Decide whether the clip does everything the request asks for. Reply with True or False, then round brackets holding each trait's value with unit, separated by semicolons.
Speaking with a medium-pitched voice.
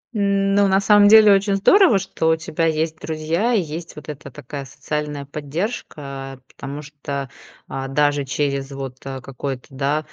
True (150 Hz)